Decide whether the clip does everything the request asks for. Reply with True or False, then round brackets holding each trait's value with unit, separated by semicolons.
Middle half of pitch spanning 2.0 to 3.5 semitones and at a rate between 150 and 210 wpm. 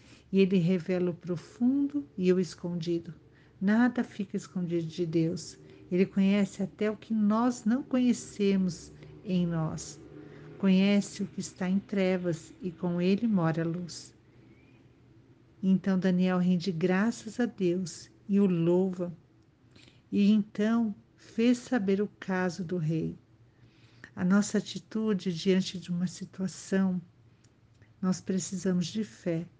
False (2.8 semitones; 125 wpm)